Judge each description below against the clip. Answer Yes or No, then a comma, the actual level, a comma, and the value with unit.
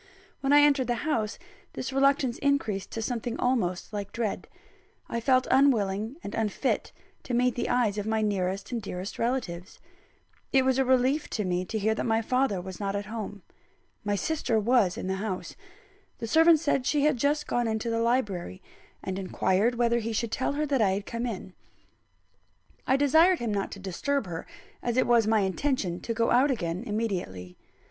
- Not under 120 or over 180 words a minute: No, average, 190 wpm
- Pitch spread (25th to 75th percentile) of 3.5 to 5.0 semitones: Yes, average, 4.5 semitones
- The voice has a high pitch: Yes, high, 230 Hz